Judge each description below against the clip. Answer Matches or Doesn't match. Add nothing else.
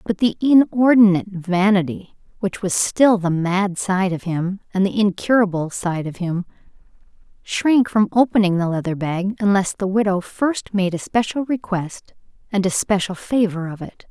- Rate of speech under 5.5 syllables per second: Matches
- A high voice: Matches